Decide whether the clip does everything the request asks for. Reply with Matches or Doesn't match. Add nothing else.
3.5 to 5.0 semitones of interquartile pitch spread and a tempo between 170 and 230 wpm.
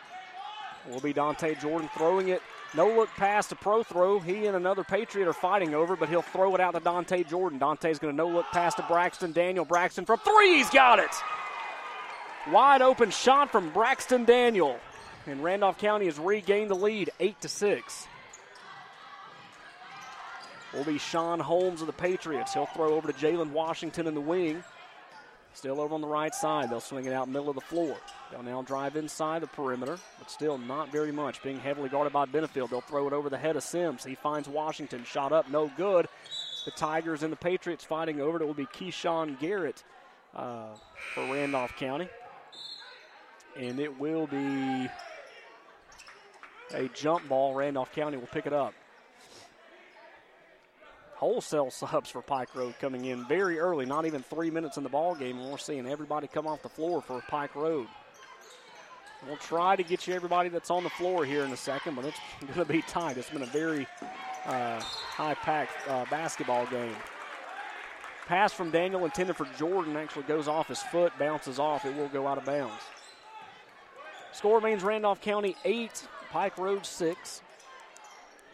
Matches